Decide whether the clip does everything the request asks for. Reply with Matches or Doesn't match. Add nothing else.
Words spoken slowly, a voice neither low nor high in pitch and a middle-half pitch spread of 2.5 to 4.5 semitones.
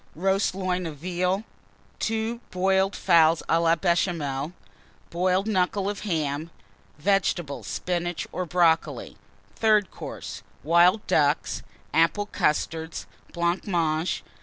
Matches